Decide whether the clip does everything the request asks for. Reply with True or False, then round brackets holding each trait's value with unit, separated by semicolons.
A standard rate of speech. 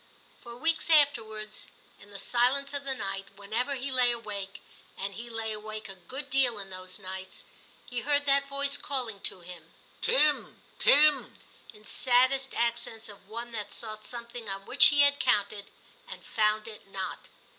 True (165 wpm)